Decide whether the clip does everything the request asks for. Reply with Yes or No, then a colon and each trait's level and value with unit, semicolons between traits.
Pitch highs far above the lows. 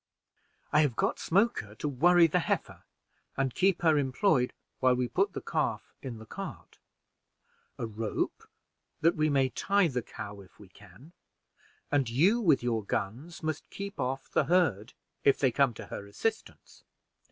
Yes: wide, 6.2 semitones